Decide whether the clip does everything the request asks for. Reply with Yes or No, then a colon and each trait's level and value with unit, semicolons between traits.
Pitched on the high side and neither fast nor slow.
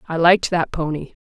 No: medium, 165 Hz; average, 195 wpm